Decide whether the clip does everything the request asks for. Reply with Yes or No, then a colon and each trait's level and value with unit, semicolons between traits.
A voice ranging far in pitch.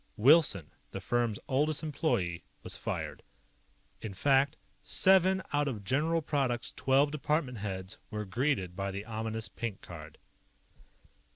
Yes: wide, 6.5 semitones